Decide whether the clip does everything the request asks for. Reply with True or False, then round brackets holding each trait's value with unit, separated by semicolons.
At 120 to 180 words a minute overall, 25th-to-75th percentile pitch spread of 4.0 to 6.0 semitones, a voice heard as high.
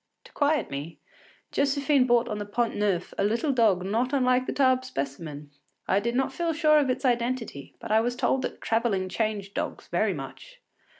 False (190 wpm; 4.7 semitones; 235 Hz)